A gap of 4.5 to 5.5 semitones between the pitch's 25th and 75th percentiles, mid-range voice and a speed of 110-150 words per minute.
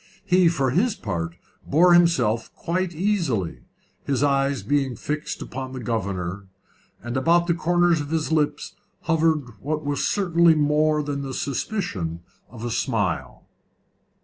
Yes: average, 5.2 semitones; medium, 145 Hz; average, 140 wpm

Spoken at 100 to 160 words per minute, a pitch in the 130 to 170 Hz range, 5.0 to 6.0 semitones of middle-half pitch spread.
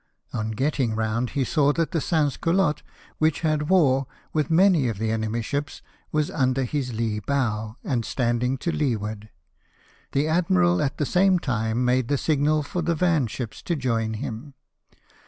No: average, 170 wpm; low, 135 Hz; wide, 5.4 semitones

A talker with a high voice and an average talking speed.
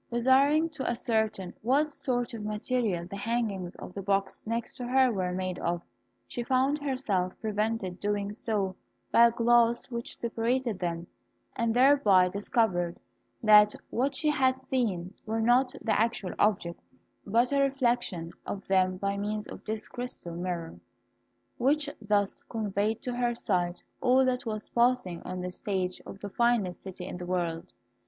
Yes: high, 220 Hz; average, 160 wpm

